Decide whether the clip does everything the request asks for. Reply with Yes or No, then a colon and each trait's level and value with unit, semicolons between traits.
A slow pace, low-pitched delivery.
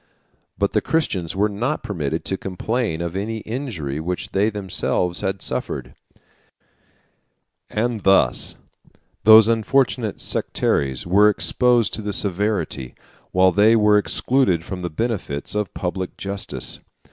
Yes: slow, 125 wpm; low, 100 Hz